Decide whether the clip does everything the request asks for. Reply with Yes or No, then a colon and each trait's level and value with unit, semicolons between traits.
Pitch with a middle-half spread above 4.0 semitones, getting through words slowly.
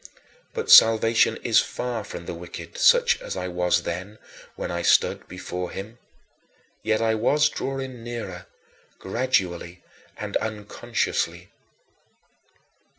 Yes: average, 5.2 semitones; slow, 115 wpm